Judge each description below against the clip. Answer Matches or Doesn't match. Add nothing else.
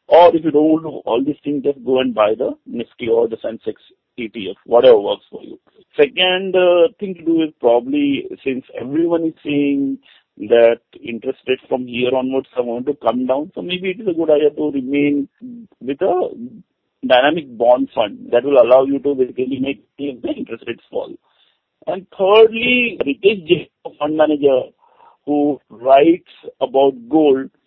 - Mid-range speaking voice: Matches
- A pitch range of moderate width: Doesn't match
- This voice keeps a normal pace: Matches